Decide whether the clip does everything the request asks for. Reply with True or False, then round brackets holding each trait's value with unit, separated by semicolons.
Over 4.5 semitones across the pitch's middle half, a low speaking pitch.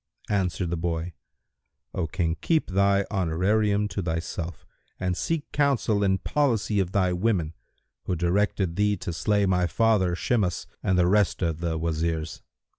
False (3.4 semitones; 95 Hz)